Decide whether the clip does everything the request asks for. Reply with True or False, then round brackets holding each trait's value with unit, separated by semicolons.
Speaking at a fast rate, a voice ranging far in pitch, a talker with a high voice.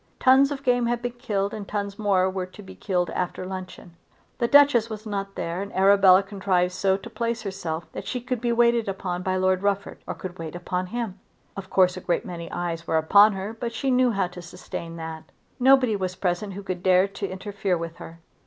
False (220 wpm; 3.6 semitones; 195 Hz)